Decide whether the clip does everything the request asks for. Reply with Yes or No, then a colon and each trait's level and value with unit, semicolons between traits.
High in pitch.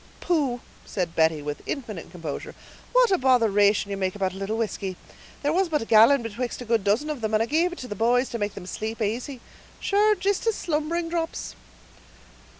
Yes: high, 230 Hz